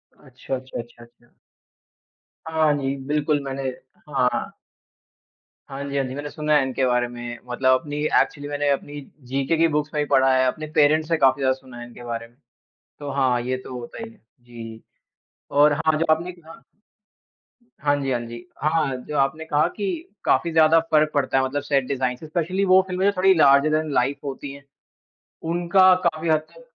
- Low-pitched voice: No, medium, 145 Hz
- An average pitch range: Yes, average, 3.3 semitones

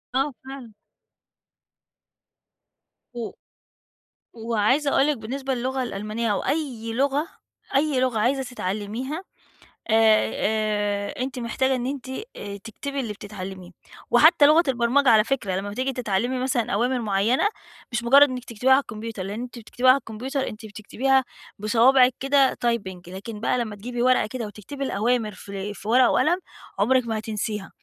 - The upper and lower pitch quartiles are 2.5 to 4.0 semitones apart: Yes, average, 3.7 semitones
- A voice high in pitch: Yes, high, 235 Hz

